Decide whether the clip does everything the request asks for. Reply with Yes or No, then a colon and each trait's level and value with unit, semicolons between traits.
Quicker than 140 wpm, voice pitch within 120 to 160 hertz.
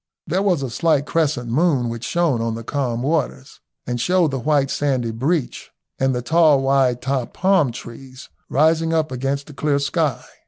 Yes: average, 180 wpm; medium, 140 Hz